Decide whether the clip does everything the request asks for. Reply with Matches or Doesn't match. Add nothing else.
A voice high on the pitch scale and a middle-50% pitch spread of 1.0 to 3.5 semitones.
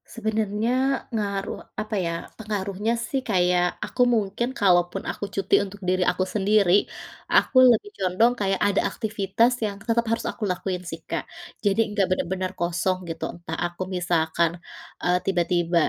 Matches